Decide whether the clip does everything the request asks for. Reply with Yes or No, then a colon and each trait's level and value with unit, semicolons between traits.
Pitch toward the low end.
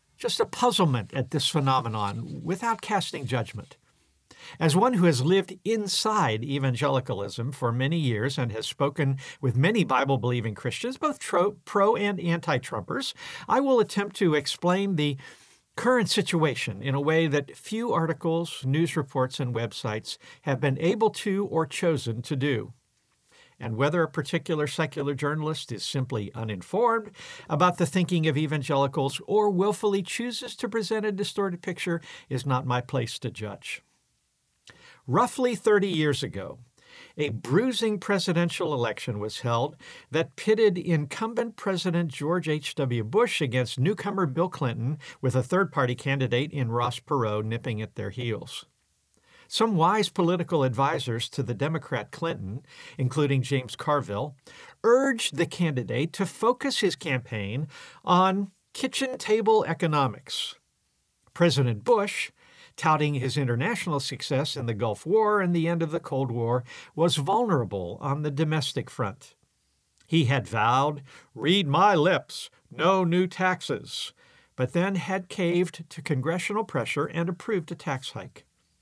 No: medium, 155 Hz